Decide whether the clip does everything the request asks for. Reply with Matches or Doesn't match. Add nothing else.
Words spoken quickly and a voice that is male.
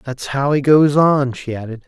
Matches